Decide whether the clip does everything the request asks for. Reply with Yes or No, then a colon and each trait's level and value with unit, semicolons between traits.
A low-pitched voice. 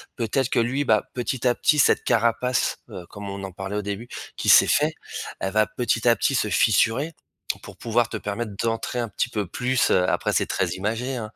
Yes: low, 115 Hz